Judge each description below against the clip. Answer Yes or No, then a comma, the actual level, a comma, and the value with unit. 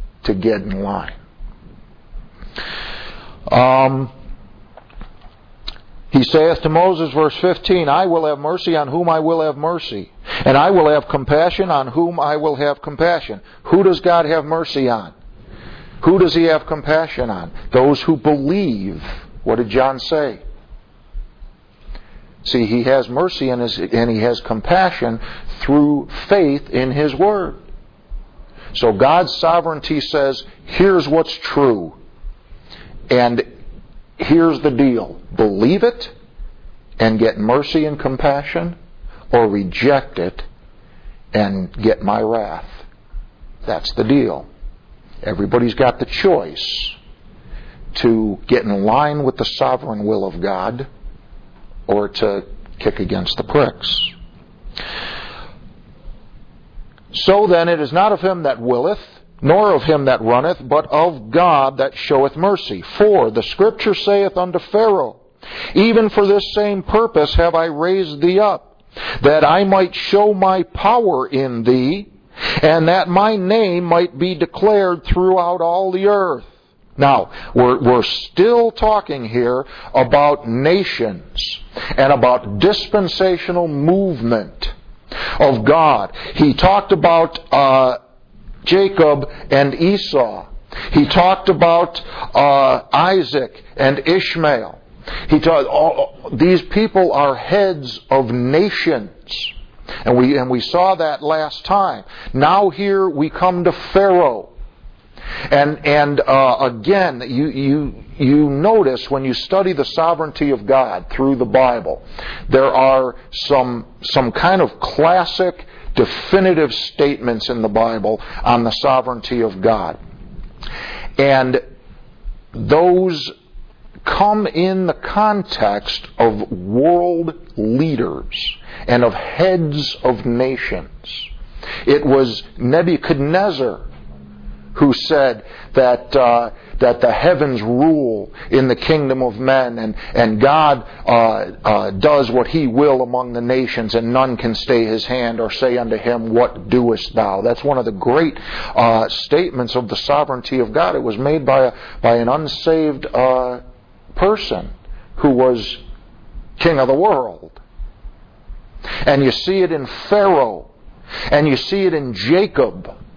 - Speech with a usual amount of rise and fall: No, wide, 6.0 semitones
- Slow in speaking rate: Yes, slow, 130 wpm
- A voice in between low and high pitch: Yes, medium, 145 Hz